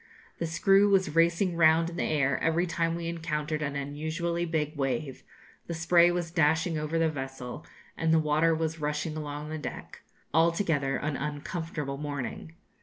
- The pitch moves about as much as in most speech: No, narrow, 2.1 semitones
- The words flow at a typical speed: Yes, average, 165 wpm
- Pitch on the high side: No, medium, 160 Hz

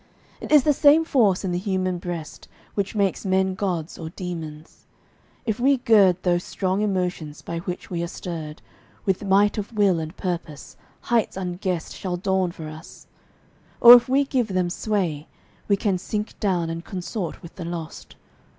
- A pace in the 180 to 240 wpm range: No, average, 170 wpm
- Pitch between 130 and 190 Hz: Yes, medium, 185 Hz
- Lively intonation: No, average, 3.2 semitones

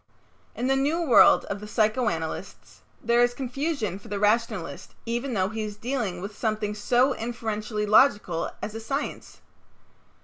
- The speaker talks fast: No, average, 150 wpm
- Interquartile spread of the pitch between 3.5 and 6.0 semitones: No, average, 3.1 semitones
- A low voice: No, high, 220 Hz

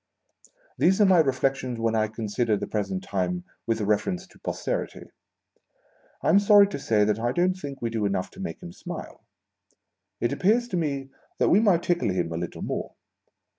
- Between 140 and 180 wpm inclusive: No, average, 190 wpm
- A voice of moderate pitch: No, low, 130 Hz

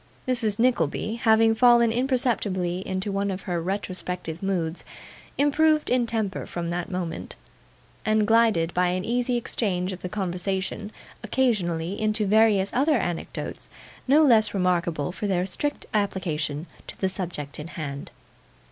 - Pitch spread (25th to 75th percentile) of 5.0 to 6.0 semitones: No, average, 4.2 semitones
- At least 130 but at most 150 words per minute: Yes, average, 140 wpm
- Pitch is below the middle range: No, high, 195 Hz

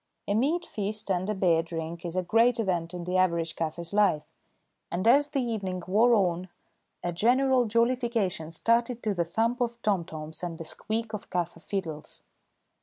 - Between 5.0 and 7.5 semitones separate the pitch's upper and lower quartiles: Yes, average, 5.3 semitones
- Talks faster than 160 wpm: Yes, average, 175 wpm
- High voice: Yes, high, 195 Hz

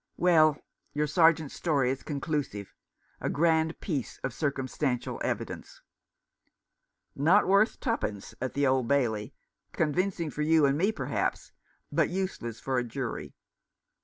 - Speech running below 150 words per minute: Yes, slow, 135 wpm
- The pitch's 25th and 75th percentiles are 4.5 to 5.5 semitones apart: No, average, 4.1 semitones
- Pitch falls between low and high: Yes, medium, 150 Hz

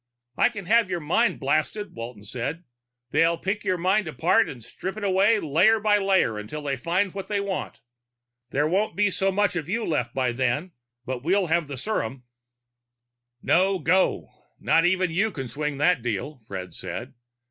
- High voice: No, medium, 170 Hz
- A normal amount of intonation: No, wide, 6.3 semitones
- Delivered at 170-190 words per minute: Yes, average, 175 wpm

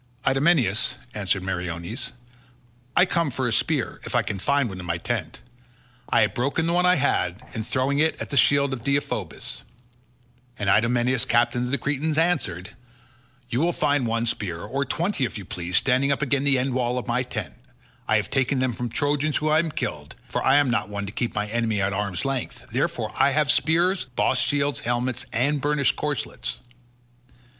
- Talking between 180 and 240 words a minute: Yes, average, 195 wpm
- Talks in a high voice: No, low, 130 Hz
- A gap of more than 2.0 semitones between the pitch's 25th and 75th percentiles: Yes, average, 4.4 semitones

